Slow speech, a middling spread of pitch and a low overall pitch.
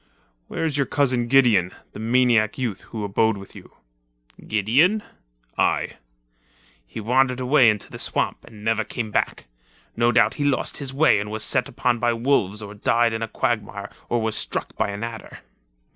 No: average, 175 wpm; average, 3.0 semitones; low, 115 Hz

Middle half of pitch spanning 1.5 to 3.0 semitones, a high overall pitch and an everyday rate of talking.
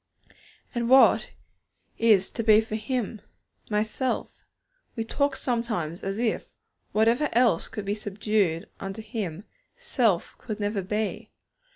No: average, 2.7 semitones; high, 215 Hz; slow, 130 wpm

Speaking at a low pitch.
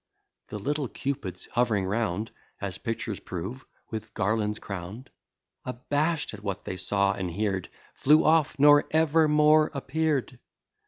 Yes: low, 115 Hz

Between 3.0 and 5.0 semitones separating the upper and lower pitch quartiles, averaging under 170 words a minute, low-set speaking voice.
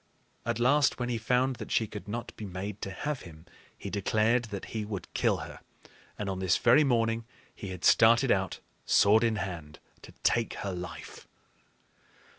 No: average, 3.6 semitones; average, 180 wpm; low, 110 Hz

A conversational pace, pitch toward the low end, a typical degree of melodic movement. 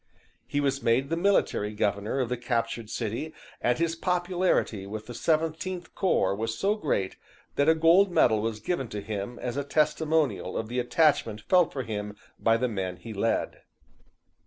No: average, 175 wpm; low, 125 Hz; wide, 6.8 semitones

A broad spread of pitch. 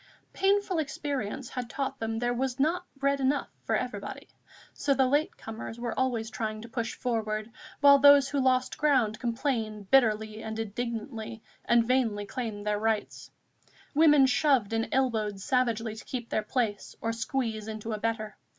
No: average, 3.5 semitones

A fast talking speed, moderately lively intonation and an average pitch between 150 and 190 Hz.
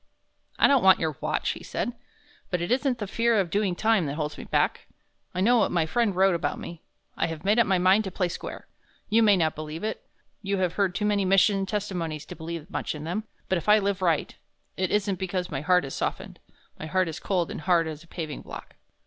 Yes: fast, 235 wpm; average, 3.8 semitones; medium, 185 Hz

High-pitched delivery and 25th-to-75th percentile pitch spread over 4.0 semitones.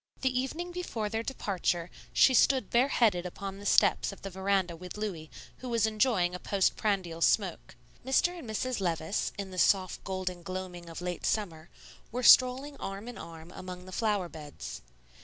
Yes: high, 195 Hz; average, 4.7 semitones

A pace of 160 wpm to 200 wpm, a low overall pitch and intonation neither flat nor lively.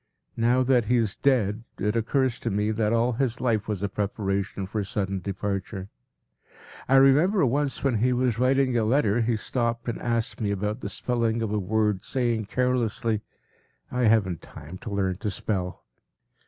Yes: average, 175 wpm; low, 115 Hz; average, 3.4 semitones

